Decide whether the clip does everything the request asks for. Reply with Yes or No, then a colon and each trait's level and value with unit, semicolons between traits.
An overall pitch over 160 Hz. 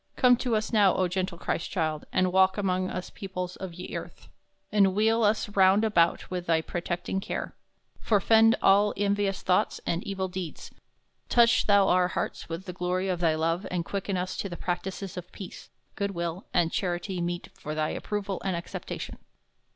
Yes: medium, 185 Hz